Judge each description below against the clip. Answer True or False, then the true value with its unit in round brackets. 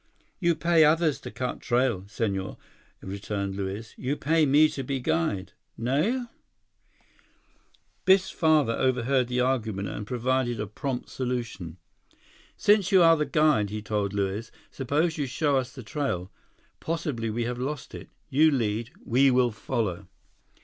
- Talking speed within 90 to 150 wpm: True (145 wpm)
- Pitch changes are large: True (5.7 semitones)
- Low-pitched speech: True (125 Hz)